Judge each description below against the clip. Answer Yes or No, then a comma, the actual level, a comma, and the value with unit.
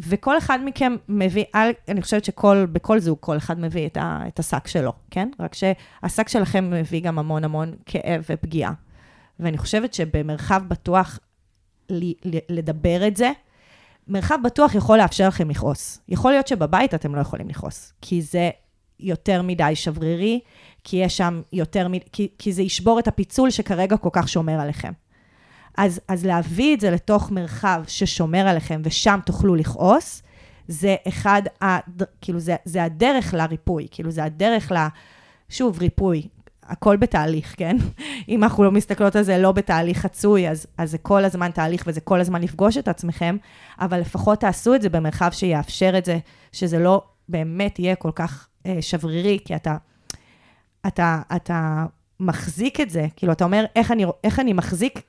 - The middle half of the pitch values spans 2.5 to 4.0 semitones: Yes, average, 3.4 semitones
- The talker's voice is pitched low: No, medium, 180 Hz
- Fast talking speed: Yes, fast, 160 wpm